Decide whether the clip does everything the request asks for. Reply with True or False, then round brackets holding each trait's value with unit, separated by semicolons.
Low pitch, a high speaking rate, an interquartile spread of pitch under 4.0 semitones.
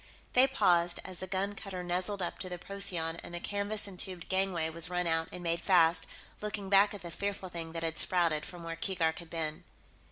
False (180 Hz; 215 wpm; 2.8 semitones)